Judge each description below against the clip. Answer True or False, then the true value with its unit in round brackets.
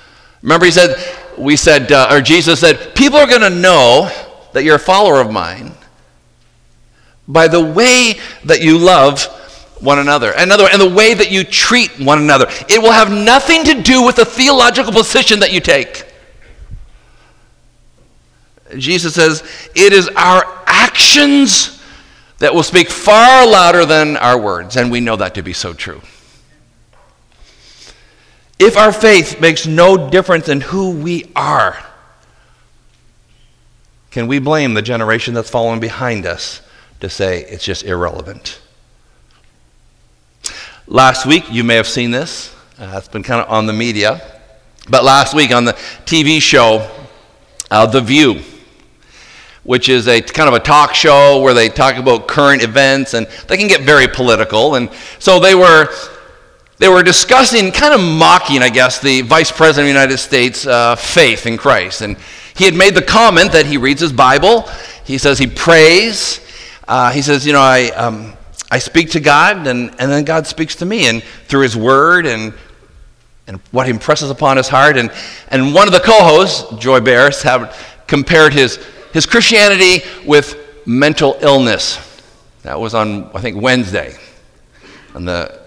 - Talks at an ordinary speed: True (160 wpm)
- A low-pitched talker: False (145 Hz)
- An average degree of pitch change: False (6.8 semitones)